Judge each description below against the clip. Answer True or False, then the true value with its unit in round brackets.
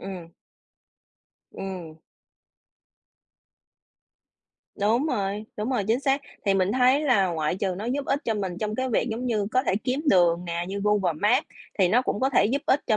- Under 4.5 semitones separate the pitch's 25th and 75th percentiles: False (5.1 semitones)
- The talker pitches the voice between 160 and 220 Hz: True (210 Hz)